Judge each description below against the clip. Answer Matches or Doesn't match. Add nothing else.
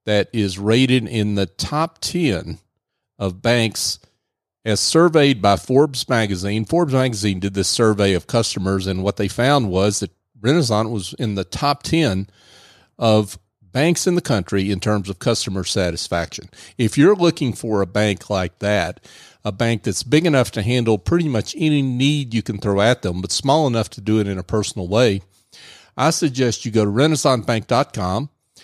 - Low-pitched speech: Matches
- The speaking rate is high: Doesn't match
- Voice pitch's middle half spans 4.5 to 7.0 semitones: Matches